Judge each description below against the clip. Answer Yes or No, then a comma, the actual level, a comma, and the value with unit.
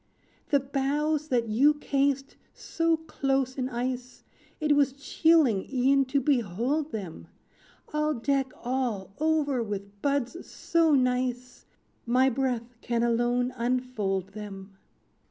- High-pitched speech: Yes, very high, 255 Hz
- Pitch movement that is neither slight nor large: Yes, average, 3.2 semitones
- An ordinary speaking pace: No, slow, 120 wpm